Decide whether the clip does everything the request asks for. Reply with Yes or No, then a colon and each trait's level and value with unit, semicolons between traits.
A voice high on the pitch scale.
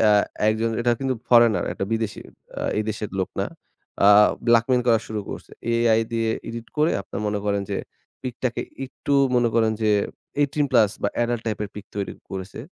No: low, 115 Hz